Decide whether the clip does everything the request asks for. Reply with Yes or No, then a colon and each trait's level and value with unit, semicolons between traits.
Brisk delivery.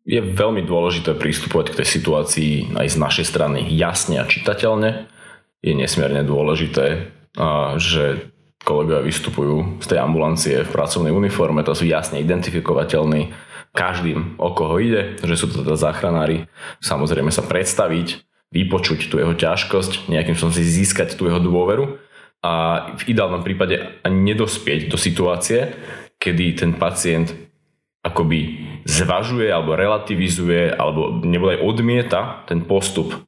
No: average, 135 wpm